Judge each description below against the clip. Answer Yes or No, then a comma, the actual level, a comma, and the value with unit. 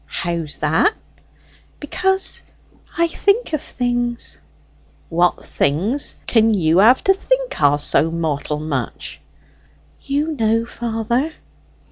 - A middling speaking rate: No, slow, 105 wpm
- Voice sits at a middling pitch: No, high, 225 Hz